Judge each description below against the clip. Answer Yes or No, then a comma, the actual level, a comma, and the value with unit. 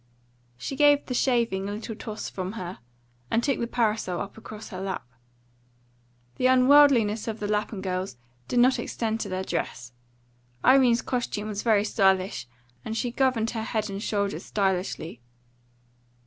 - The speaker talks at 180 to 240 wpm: No, average, 155 wpm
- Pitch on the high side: Yes, high, 215 Hz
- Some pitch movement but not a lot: Yes, average, 3.7 semitones